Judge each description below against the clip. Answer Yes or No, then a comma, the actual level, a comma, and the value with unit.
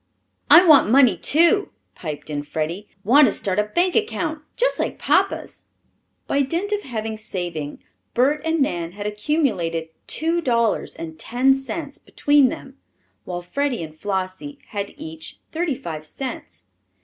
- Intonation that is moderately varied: No, wide, 9.0 semitones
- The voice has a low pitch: No, high, 240 Hz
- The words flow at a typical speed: Yes, average, 150 wpm